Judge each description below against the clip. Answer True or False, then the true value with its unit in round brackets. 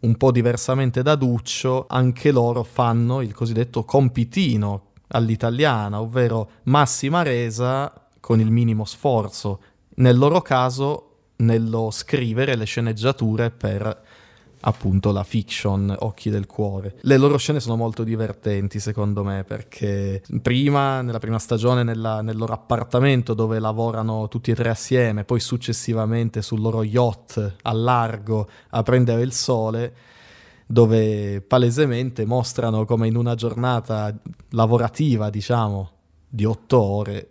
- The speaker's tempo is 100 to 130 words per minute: True (125 wpm)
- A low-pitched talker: True (115 Hz)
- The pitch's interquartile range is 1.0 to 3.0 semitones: True (2.4 semitones)